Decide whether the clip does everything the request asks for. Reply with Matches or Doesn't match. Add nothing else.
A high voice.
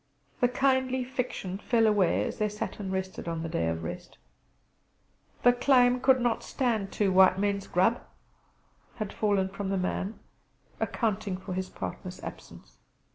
Matches